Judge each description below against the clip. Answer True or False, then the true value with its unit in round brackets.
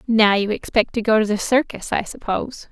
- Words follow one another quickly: True (220 wpm)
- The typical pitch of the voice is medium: False (220 Hz)